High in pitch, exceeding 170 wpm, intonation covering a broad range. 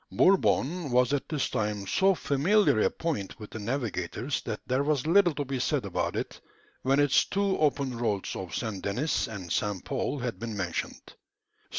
No: low, 130 Hz; average, 180 wpm; wide, 6.1 semitones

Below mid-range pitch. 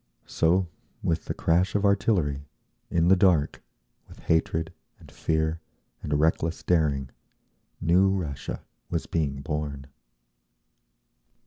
Yes: very low, 80 Hz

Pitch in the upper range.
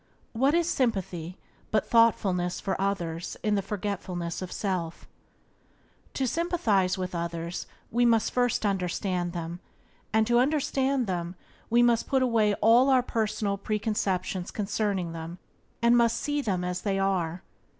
Yes: high, 200 Hz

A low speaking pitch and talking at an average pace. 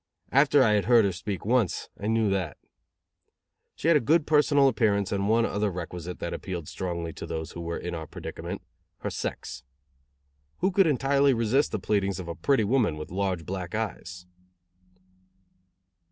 Yes: low, 100 Hz; average, 170 wpm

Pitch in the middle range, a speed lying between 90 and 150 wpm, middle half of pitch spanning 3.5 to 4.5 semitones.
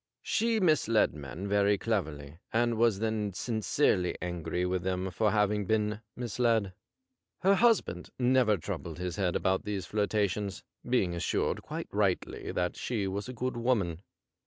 No: low, 105 Hz; average, 145 wpm; average, 4.2 semitones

